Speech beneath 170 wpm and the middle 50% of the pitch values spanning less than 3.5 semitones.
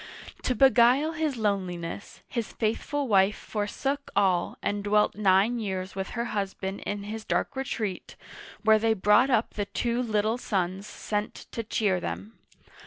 Yes: average, 150 wpm; average, 3.1 semitones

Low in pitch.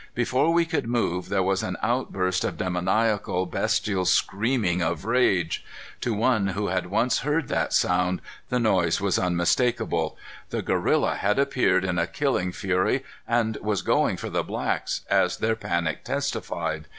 Yes: low, 100 Hz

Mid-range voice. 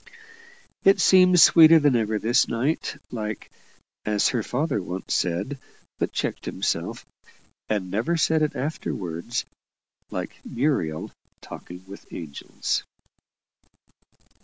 No: low, 115 Hz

